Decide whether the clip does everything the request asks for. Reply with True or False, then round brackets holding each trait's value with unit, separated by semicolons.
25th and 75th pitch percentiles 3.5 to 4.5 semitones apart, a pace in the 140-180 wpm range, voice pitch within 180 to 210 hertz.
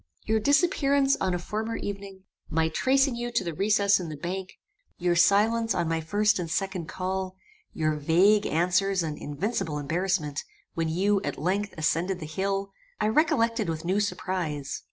True (4.1 semitones; 165 wpm; 190 Hz)